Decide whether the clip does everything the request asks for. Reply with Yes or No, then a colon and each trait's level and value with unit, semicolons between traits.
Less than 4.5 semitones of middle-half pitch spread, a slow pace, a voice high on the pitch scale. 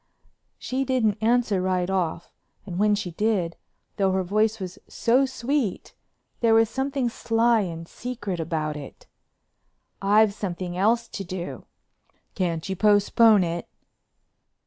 Yes: average, 4.1 semitones; slow, 130 wpm; high, 205 Hz